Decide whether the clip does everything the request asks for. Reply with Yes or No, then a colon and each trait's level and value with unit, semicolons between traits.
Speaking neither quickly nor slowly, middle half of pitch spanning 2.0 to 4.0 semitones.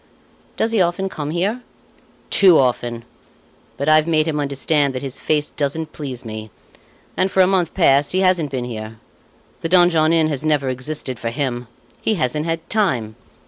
No: average, 175 wpm; average, 4.8 semitones